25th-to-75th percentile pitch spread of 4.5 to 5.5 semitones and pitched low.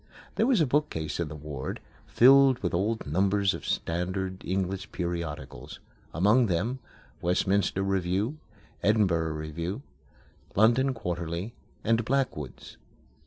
Yes: average, 5.1 semitones; very low, 95 Hz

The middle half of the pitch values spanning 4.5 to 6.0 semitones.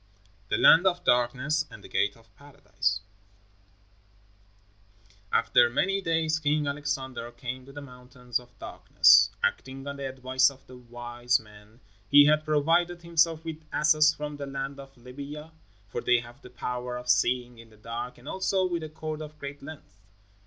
No: average, 3.8 semitones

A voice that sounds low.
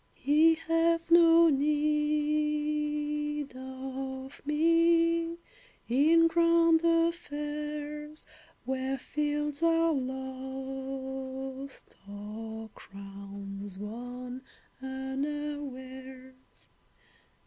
No: very high, 290 Hz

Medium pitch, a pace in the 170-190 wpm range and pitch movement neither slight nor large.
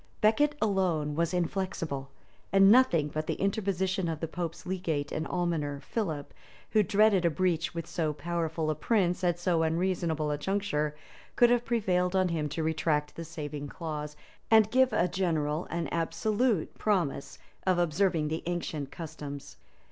No: medium, 170 Hz; average, 155 wpm; average, 3.7 semitones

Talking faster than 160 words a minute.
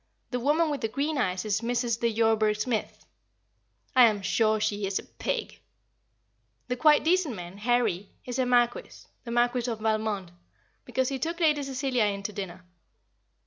Yes: average, 170 wpm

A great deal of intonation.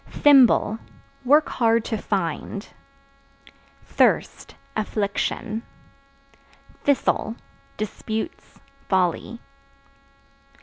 No: average, 3.2 semitones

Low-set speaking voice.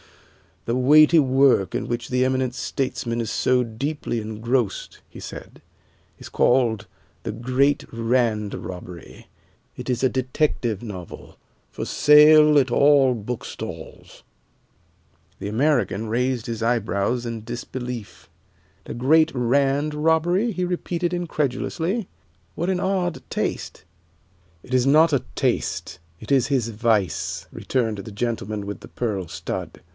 Yes: low, 125 Hz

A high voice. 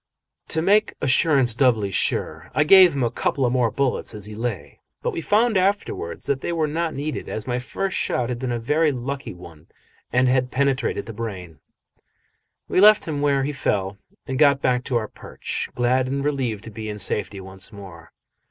No: low, 130 Hz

